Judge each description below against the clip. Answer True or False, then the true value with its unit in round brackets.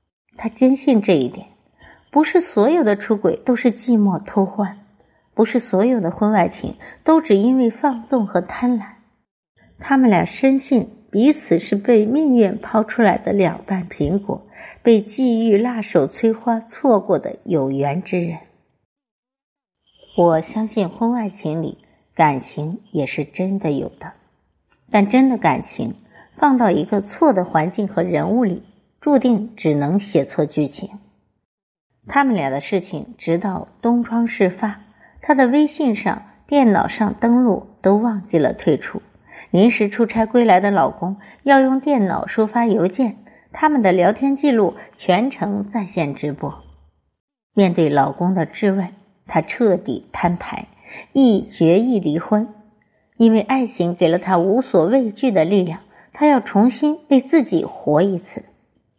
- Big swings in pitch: False (5.0 semitones)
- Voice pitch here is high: True (210 Hz)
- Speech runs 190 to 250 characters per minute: True (210 characters per minute)